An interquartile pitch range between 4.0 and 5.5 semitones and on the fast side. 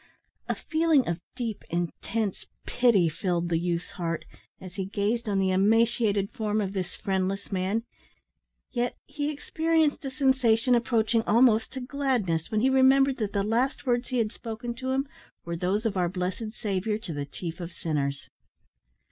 No: average, 5.1 semitones; average, 165 wpm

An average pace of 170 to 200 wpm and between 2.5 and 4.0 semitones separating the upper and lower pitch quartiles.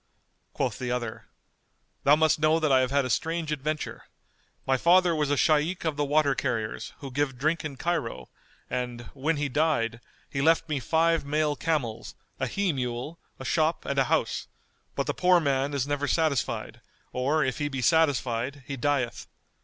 Yes: average, 180 wpm; average, 3.4 semitones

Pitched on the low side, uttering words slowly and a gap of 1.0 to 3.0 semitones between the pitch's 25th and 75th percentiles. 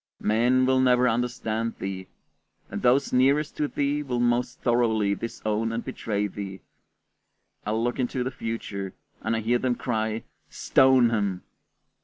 No: low, 120 Hz; average, 145 wpm; average, 2.7 semitones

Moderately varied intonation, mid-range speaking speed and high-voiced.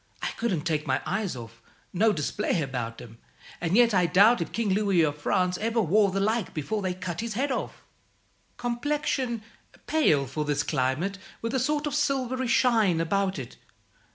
No: wide, 7.3 semitones; average, 180 wpm; high, 195 Hz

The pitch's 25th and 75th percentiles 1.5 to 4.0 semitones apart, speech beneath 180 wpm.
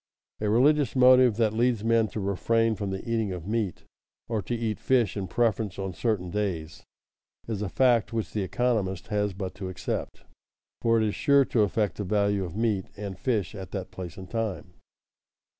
No: average, 3.1 semitones; average, 190 wpm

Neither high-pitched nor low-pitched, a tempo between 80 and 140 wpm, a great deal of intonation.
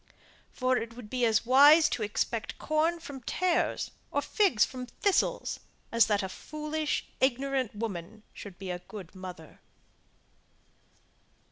No: high, 245 Hz; slow, 135 wpm; wide, 6.1 semitones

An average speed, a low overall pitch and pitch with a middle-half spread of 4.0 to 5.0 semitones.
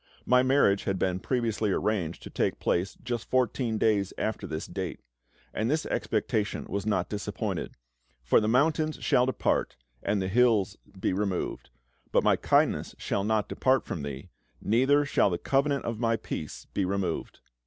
Yes: average, 165 wpm; low, 105 Hz; average, 4.6 semitones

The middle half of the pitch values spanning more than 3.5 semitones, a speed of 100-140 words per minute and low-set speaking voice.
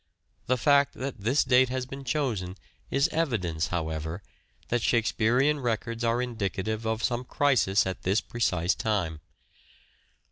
Yes: average, 5.2 semitones; slow, 135 wpm; low, 115 Hz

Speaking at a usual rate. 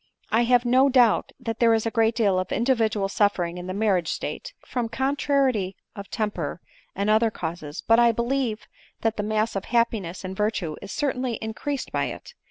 Yes: average, 185 wpm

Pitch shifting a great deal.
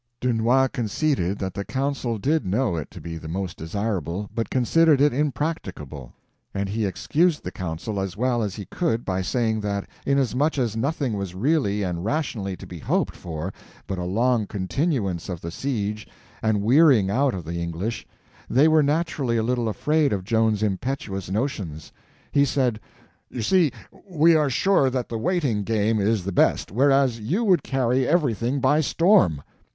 Yes: wide, 6.1 semitones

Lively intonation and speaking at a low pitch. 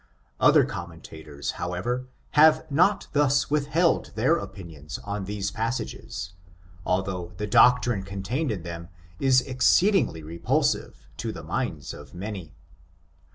Yes: wide, 7.3 semitones; low, 100 Hz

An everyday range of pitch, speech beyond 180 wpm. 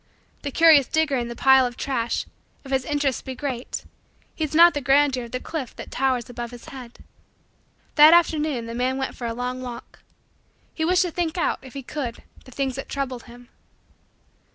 Yes: average, 3.2 semitones; average, 195 wpm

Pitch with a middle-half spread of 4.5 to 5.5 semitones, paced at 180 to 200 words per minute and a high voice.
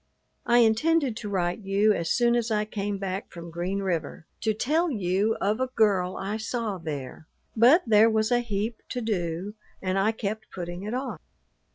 No: average, 3.6 semitones; average, 185 wpm; high, 210 Hz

